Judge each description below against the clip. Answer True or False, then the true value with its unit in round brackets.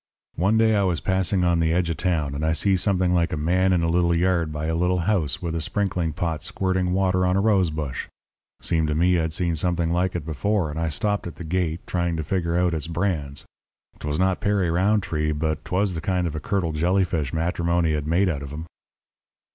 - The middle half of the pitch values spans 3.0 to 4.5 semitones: False (2.5 semitones)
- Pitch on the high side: False (85 Hz)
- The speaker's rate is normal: False (225 wpm)